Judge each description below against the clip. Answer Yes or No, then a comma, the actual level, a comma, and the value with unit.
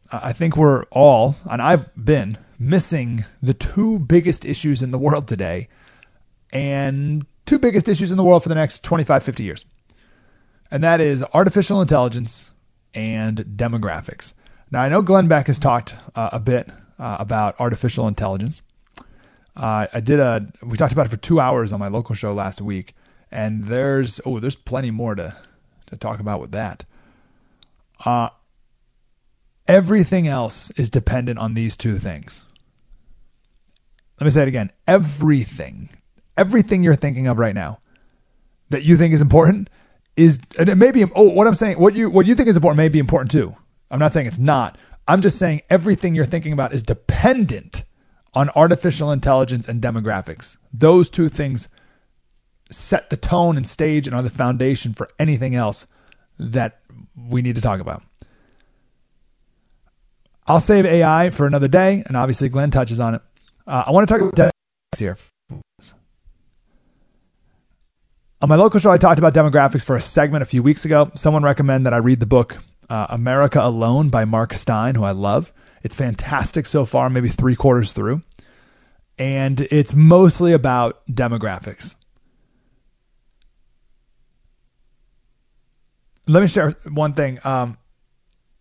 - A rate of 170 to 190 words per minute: No, average, 160 wpm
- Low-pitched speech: Yes, low, 130 Hz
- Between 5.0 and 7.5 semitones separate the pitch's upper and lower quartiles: Yes, wide, 5.6 semitones